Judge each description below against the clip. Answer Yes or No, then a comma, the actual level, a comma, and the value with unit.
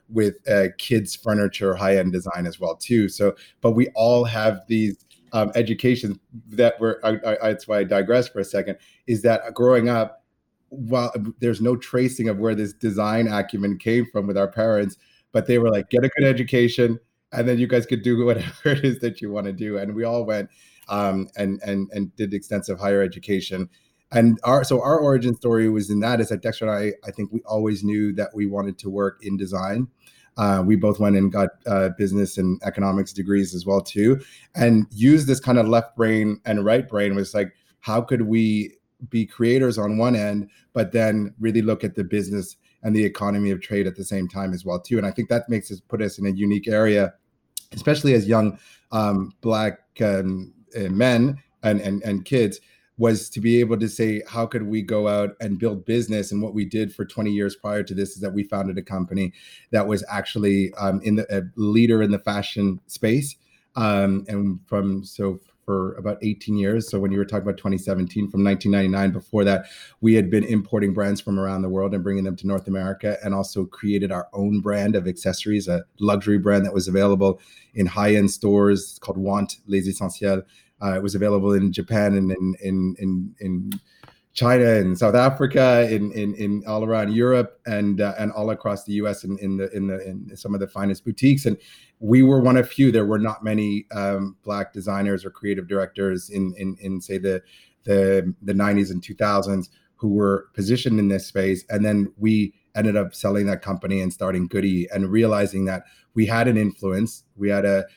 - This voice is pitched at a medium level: No, low, 105 Hz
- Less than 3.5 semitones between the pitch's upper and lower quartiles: Yes, narrow, 2.4 semitones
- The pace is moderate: No, fast, 210 wpm